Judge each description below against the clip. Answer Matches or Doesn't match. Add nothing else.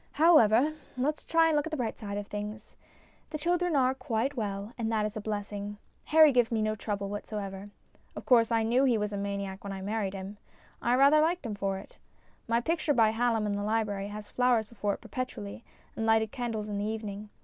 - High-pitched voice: Matches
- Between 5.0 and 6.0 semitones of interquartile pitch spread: Doesn't match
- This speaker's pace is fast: Matches